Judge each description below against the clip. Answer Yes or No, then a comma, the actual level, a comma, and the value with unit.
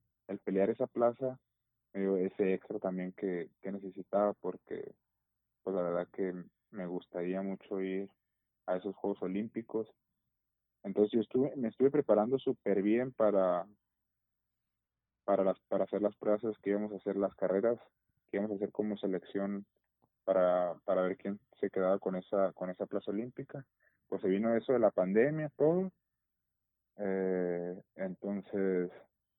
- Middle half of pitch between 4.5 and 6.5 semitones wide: No, average, 2.8 semitones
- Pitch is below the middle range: Yes, low, 100 Hz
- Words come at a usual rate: Yes, average, 145 wpm